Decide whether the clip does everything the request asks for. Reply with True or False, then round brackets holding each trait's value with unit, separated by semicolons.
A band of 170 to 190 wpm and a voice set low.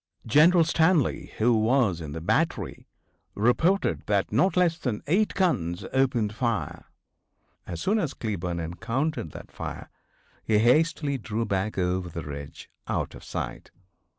False (140 wpm; 115 Hz)